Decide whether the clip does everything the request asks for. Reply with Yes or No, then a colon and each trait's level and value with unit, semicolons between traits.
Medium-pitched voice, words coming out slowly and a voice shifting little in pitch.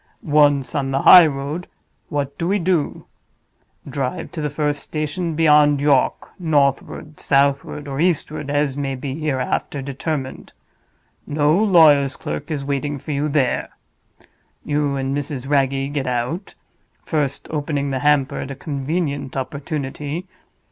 Yes: medium, 145 Hz; slow, 130 wpm; narrow, 1.9 semitones